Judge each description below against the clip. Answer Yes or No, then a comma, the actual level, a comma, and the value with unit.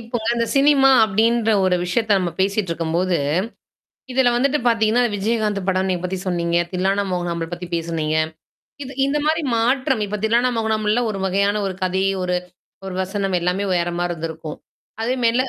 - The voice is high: Yes, high, 200 Hz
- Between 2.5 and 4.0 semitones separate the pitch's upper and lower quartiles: No, average, 4.4 semitones